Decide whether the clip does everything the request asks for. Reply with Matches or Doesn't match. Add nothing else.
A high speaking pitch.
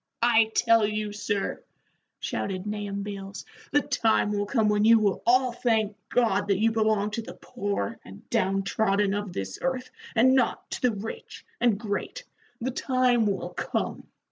Matches